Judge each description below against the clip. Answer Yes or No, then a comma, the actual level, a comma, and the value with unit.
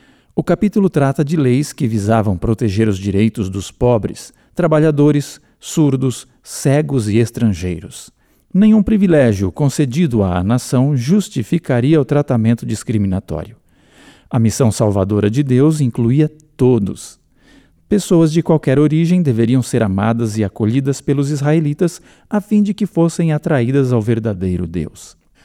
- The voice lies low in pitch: Yes, low, 130 Hz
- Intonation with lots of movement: Yes, wide, 5.8 semitones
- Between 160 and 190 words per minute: No, average, 125 wpm